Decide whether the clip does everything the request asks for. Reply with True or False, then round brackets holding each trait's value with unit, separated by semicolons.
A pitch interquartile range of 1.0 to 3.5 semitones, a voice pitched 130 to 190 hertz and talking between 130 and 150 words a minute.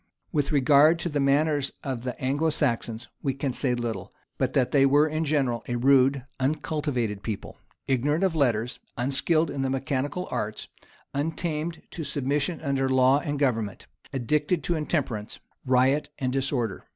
False (3.0 semitones; 140 Hz; 160 wpm)